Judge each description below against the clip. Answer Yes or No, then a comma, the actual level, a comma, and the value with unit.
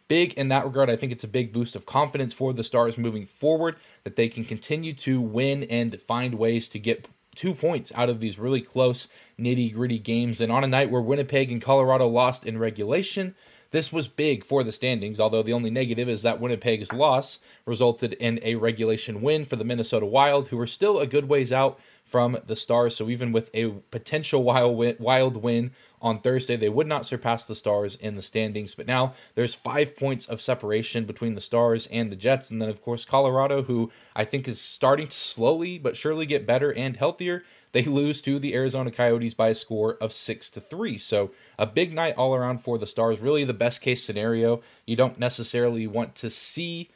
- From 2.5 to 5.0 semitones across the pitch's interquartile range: Yes, average, 2.9 semitones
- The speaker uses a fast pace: Yes, fast, 210 wpm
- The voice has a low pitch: Yes, low, 120 Hz